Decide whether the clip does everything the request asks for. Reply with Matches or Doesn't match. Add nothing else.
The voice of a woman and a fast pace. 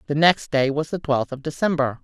Matches